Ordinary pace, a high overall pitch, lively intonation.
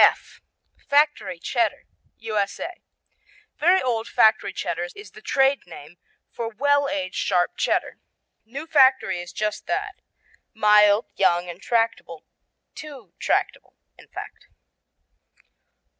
No: slow, 115 wpm; high, 220 Hz; wide, 6.4 semitones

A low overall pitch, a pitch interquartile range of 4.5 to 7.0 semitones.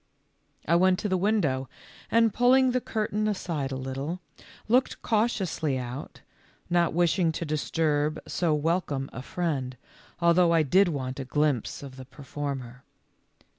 No: medium, 160 Hz; wide, 5.6 semitones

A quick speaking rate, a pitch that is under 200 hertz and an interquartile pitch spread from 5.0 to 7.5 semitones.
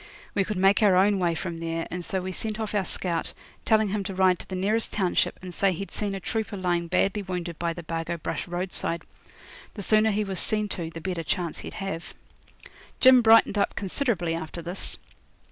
No: fast, 210 wpm; medium, 185 Hz; average, 3.2 semitones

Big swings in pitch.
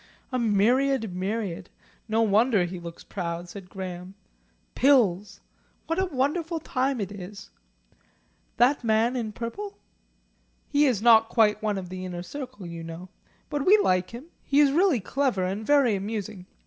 Yes: wide, 6.1 semitones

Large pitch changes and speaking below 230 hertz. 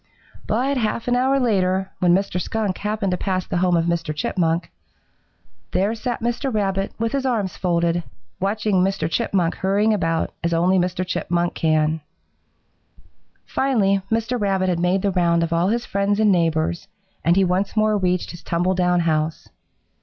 No: average, 3.6 semitones; medium, 185 Hz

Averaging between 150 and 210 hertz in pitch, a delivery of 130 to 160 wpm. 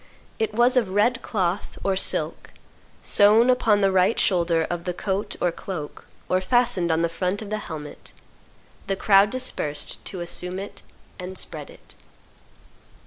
Yes: high, 190 Hz; average, 155 wpm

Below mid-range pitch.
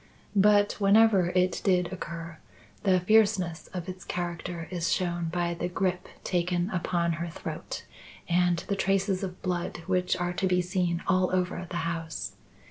No: medium, 180 Hz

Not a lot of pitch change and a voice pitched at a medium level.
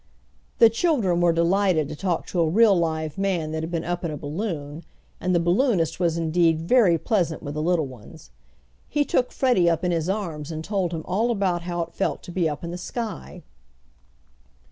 No: average, 3.4 semitones; medium, 175 Hz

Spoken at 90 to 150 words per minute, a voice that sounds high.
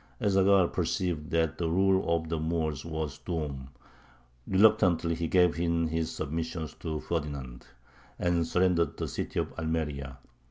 No: average, 145 wpm; very low, 80 Hz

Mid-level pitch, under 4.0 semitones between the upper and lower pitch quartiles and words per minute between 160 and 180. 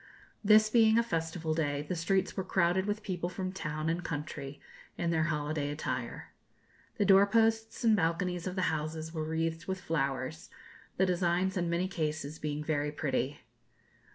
Yes: medium, 165 Hz; average, 3.6 semitones; average, 165 wpm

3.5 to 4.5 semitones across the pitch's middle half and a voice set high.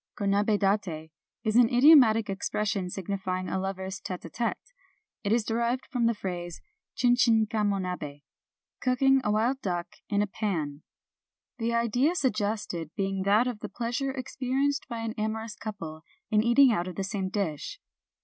Yes: average, 3.8 semitones; high, 210 Hz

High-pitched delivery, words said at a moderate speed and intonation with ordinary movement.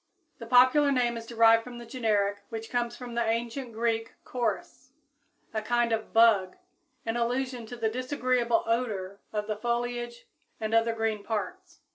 No: high, 235 Hz; average, 160 wpm; narrow, 1.6 semitones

